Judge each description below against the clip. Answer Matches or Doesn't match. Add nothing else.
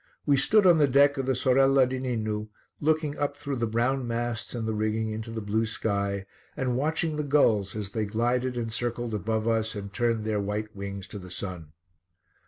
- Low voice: Matches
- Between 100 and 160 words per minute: Doesn't match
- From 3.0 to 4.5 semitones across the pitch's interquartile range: Matches